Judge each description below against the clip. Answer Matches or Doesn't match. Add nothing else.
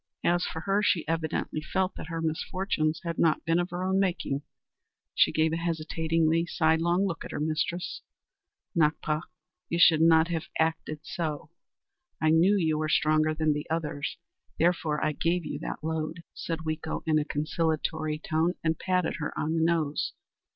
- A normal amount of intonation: Doesn't match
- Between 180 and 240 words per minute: Doesn't match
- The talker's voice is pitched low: Doesn't match